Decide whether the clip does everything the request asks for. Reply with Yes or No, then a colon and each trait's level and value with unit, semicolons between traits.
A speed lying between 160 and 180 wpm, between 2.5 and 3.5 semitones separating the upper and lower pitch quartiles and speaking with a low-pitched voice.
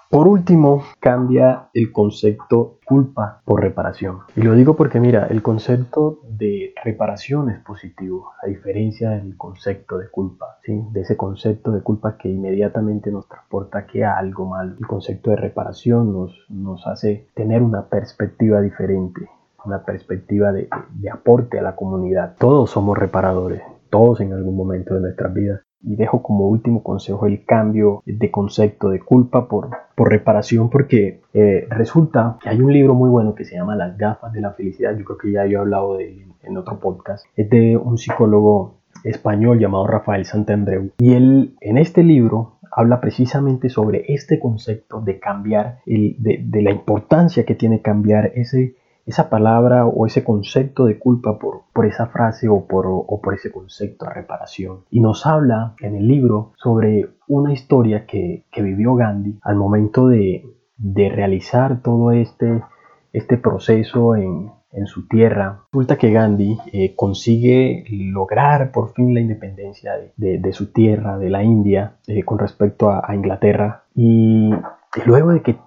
Yes: average, 170 wpm; average, 3.1 semitones; low, 110 Hz